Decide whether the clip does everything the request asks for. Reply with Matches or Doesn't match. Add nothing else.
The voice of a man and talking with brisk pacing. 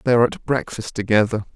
Doesn't match